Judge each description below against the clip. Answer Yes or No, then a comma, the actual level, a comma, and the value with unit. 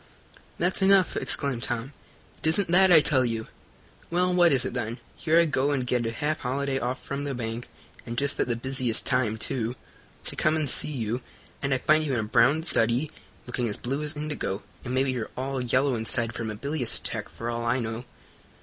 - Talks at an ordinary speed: No, fast, 215 wpm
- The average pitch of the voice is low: Yes, low, 130 Hz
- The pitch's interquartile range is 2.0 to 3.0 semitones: No, average, 4.0 semitones